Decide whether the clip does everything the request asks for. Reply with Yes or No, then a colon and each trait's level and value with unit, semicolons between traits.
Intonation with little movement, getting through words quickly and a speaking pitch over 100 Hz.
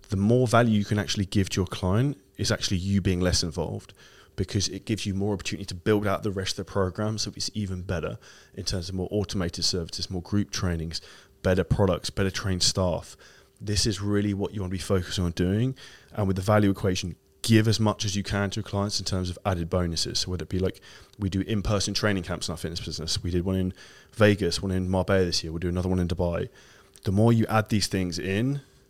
No: narrow, 2.3 semitones; fast, 240 wpm; very low, 95 Hz